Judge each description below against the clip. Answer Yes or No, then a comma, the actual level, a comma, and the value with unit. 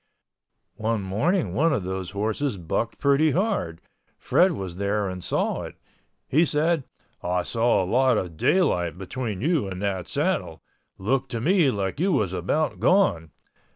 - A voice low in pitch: Yes, low, 110 Hz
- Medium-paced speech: Yes, average, 155 wpm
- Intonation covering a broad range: Yes, wide, 8.1 semitones